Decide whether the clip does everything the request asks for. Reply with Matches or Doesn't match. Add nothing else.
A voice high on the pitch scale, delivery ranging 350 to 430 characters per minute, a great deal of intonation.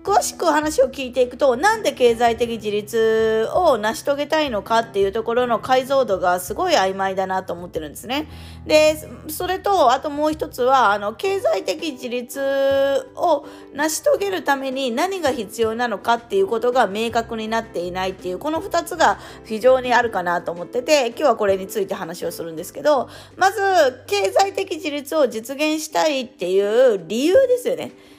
Matches